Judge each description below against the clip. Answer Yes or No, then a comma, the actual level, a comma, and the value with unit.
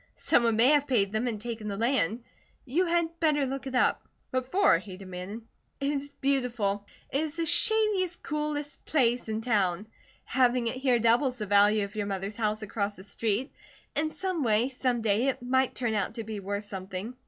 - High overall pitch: Yes, high, 240 Hz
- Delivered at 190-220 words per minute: Yes, average, 195 wpm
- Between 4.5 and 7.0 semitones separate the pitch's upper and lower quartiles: Yes, average, 4.9 semitones